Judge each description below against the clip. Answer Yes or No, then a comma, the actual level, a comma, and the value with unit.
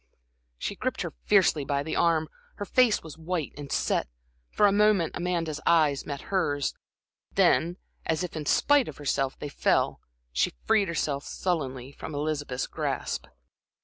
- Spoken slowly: No, average, 155 wpm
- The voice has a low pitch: No, medium, 155 Hz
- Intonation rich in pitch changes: No, average, 3.9 semitones